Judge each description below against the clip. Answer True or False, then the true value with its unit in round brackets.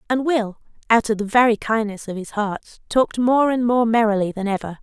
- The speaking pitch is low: False (225 Hz)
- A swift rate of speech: True (210 wpm)